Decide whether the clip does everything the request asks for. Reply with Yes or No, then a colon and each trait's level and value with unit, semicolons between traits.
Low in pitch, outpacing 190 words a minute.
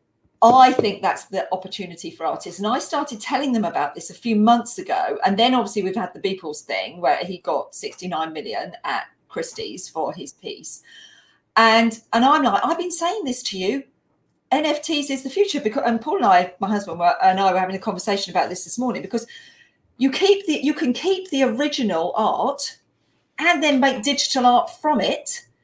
No: high, 245 Hz; average, 200 wpm